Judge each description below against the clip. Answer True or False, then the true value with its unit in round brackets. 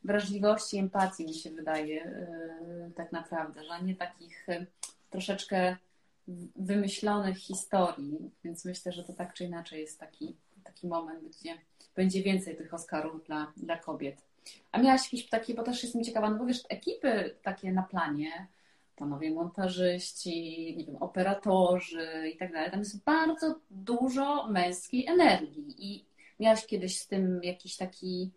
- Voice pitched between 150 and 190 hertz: True (185 Hz)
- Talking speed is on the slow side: False (145 wpm)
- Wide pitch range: False (3.6 semitones)